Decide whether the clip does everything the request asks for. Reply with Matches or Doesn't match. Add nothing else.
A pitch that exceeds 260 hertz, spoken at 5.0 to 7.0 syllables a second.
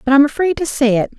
Matches